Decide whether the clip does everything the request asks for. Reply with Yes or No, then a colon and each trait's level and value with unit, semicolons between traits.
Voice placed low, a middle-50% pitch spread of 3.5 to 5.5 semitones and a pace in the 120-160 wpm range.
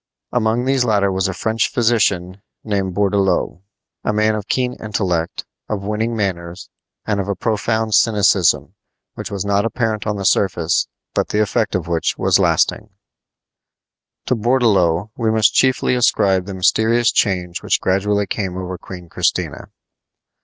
No: low, 100 Hz; average, 3.0 semitones; average, 150 wpm